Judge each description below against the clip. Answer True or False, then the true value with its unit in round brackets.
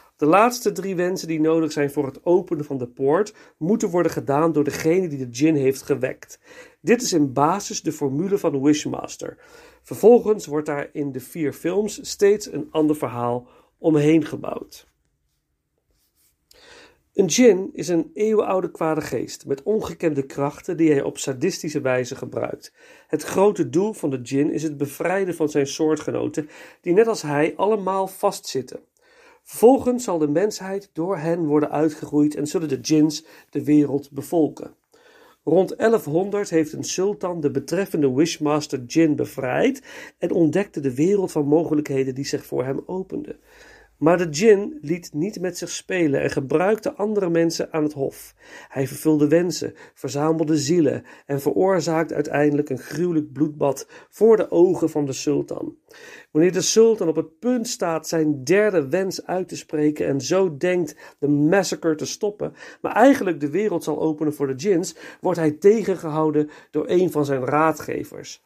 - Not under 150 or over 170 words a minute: True (160 wpm)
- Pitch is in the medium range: True (160 Hz)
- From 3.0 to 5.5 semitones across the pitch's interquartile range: True (4.5 semitones)